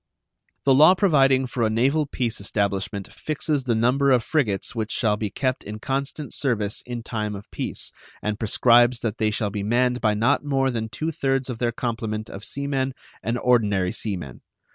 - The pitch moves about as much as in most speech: Yes, average, 3.9 semitones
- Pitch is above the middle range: No, low, 120 Hz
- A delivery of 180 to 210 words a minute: Yes, average, 190 wpm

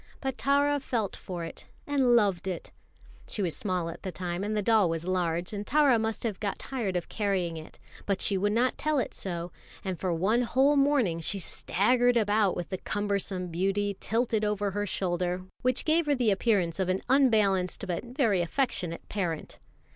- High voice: Yes, high, 205 Hz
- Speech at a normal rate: Yes, average, 190 wpm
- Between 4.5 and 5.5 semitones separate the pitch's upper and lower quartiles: Yes, average, 4.9 semitones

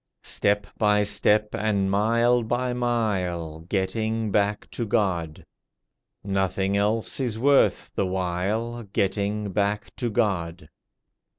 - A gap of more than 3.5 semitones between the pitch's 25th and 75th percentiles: No, average, 2.7 semitones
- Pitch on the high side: No, low, 105 Hz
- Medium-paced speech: No, slow, 110 wpm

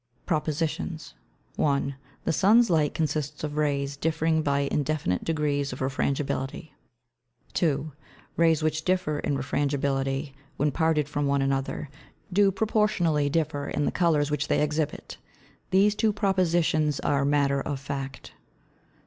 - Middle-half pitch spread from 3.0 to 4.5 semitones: No, narrow, 2.6 semitones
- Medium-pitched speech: Yes, medium, 150 Hz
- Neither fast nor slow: No, slow, 130 wpm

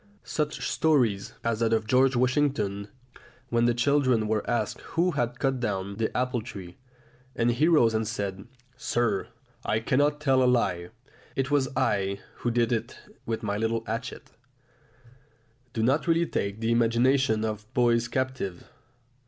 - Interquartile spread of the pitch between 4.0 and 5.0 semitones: No, average, 3.2 semitones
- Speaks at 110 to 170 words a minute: Yes, average, 155 wpm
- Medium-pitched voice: No, low, 120 Hz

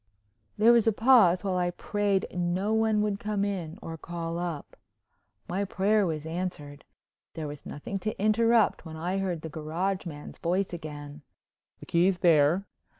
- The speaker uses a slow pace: No, average, 160 wpm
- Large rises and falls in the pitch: No, average, 3.8 semitones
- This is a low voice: No, medium, 180 Hz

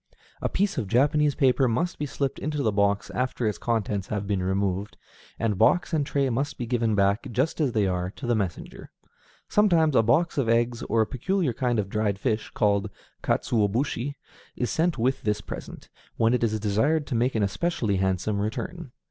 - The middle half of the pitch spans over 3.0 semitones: Yes, average, 5.2 semitones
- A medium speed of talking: Yes, average, 190 wpm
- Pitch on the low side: Yes, low, 115 Hz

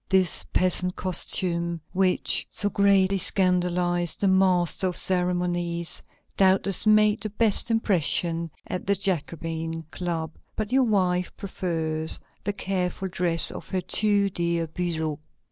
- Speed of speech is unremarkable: No, slow, 125 wpm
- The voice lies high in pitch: No, medium, 180 Hz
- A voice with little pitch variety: Yes, narrow, 2.3 semitones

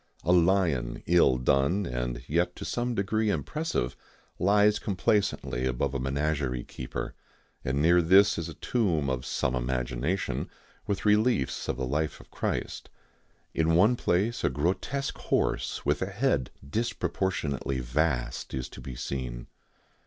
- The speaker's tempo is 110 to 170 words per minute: Yes, average, 140 wpm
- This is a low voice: Yes, very low, 80 Hz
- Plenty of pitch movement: Yes, wide, 7.4 semitones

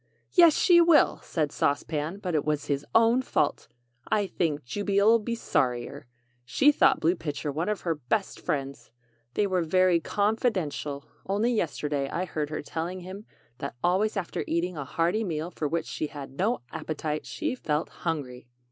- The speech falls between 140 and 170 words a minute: No, average, 180 wpm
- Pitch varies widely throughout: Yes, wide, 5.7 semitones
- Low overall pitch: No, medium, 170 Hz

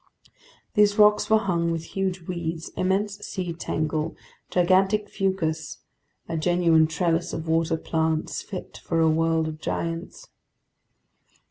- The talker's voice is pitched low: No, medium, 170 Hz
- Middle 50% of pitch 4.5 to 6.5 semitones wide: No, average, 2.8 semitones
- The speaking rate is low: Yes, slow, 120 wpm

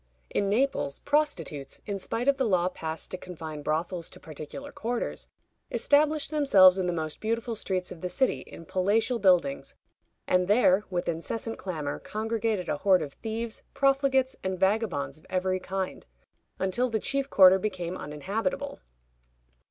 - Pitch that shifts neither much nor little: Yes, average, 4.8 semitones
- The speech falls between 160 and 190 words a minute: No, average, 150 wpm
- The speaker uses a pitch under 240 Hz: Yes, high, 190 Hz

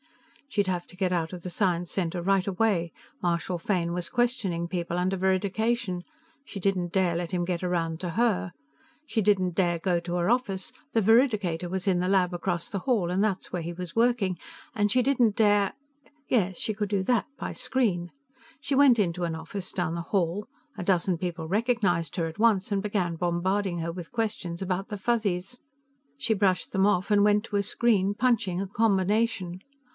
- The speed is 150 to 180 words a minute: No, average, 190 wpm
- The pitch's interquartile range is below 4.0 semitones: Yes, average, 3.1 semitones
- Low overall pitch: No, high, 190 Hz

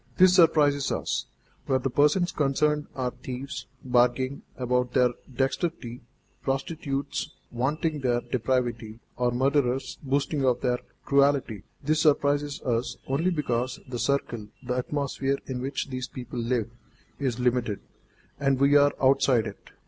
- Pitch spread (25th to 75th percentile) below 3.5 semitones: Yes, narrow, 2.5 semitones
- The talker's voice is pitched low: Yes, low, 130 Hz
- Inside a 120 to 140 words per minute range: Yes, slow, 135 wpm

